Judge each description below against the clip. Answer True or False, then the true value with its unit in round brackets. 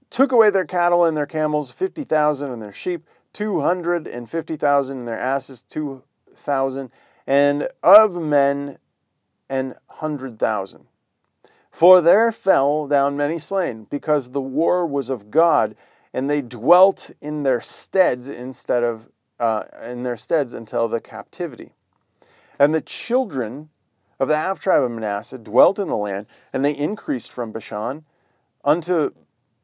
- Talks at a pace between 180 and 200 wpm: False (150 wpm)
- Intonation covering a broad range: False (5.0 semitones)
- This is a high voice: False (140 Hz)